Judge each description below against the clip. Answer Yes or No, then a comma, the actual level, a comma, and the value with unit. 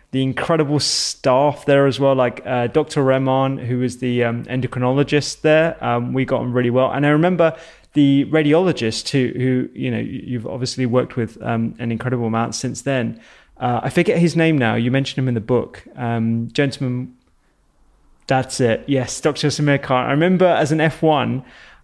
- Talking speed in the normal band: Yes, average, 180 wpm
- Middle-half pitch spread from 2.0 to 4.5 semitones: Yes, average, 3.0 semitones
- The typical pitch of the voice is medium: No, low, 130 Hz